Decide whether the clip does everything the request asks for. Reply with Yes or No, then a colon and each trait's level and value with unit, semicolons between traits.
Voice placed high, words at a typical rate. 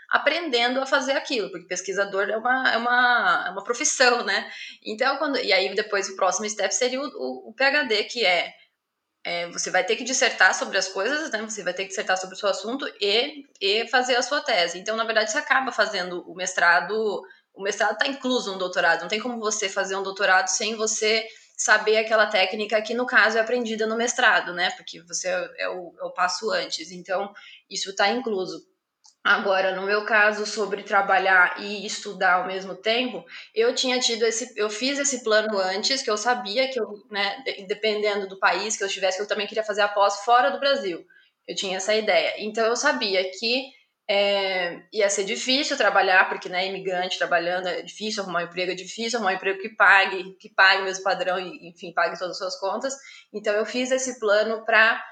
No: high, 210 Hz; fast, 210 wpm